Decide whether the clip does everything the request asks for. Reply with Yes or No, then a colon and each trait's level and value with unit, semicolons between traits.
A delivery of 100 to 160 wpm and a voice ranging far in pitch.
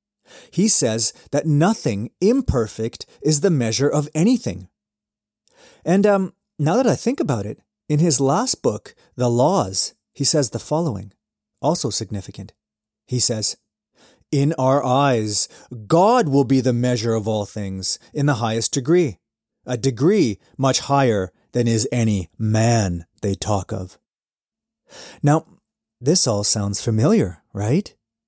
Yes: slow, 135 wpm; wide, 6.1 semitones